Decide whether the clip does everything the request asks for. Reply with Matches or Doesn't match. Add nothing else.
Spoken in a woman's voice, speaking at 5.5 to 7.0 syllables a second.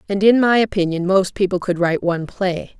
Matches